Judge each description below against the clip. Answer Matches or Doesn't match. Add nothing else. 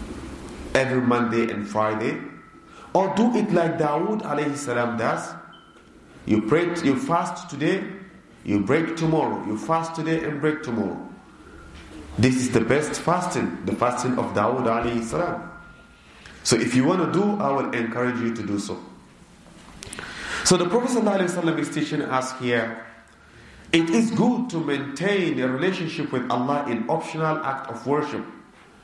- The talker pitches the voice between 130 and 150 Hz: Matches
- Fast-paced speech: Doesn't match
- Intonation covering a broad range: Matches